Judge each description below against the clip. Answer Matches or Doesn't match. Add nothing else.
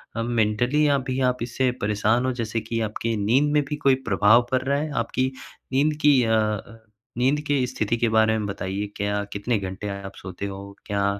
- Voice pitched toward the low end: Matches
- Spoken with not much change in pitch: Doesn't match